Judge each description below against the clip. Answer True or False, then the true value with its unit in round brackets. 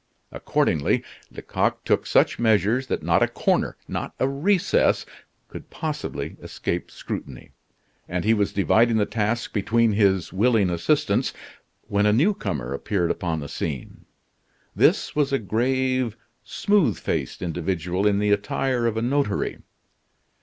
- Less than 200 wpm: True (140 wpm)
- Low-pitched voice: True (105 Hz)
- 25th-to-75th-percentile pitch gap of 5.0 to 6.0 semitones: True (5.3 semitones)